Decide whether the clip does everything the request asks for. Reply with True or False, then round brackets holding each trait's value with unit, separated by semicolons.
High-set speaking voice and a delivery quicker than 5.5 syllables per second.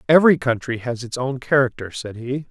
False (130 Hz; 5.7 syllables/s)